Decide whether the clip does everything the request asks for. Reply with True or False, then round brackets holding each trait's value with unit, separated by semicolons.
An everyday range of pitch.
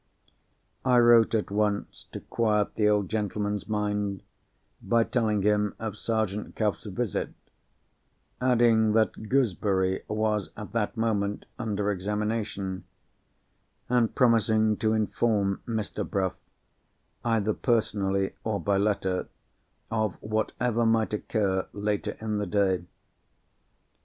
False (1.7 semitones)